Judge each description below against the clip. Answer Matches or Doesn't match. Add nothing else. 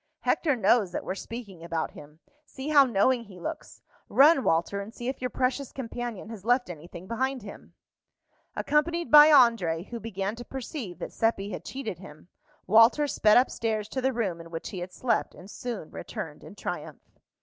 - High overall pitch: Matches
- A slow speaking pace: Doesn't match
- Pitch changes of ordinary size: Doesn't match